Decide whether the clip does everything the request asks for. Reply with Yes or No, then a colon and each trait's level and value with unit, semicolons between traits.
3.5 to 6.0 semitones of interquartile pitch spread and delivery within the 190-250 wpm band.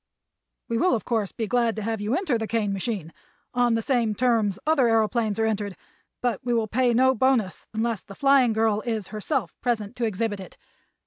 No: narrow, 2.5 semitones; average, 200 wpm